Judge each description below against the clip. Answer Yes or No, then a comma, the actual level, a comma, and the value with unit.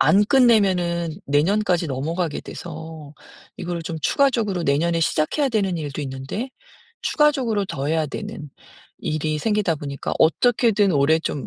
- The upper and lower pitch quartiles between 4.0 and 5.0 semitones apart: No, wide, 5.4 semitones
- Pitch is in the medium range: Yes, medium, 170 Hz